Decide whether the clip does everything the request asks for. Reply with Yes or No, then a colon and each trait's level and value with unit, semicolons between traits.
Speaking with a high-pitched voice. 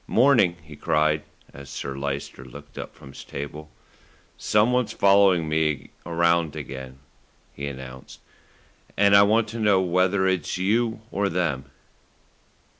No: very low, 85 Hz